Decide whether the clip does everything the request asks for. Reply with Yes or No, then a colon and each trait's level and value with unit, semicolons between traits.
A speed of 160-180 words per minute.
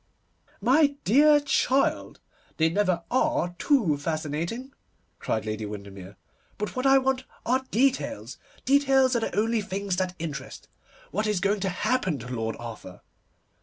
No: average, 140 wpm